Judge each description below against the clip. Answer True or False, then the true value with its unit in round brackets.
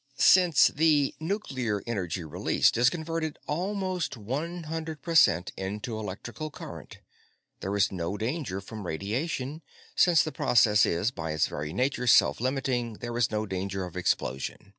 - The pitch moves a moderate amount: False (8.0 semitones)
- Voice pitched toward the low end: True (120 Hz)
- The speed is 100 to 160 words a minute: True (150 wpm)